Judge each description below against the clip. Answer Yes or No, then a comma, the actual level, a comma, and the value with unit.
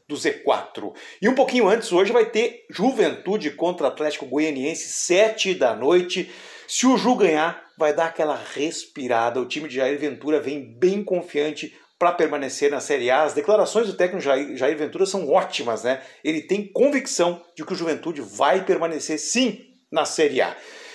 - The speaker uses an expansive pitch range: Yes, wide, 7.0 semitones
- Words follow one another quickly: No, average, 165 wpm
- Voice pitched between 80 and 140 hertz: No, medium, 175 Hz